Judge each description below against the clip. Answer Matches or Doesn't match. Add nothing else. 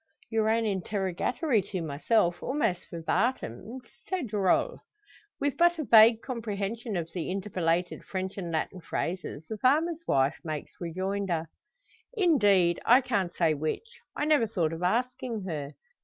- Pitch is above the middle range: Matches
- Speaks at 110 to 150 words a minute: Matches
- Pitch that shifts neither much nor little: Doesn't match